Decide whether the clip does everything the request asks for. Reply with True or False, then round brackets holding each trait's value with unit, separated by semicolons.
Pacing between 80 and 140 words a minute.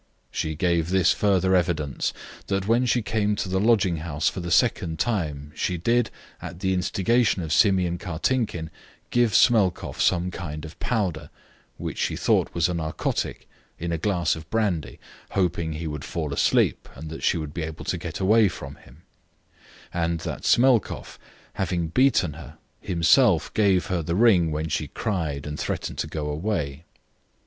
False (170 wpm)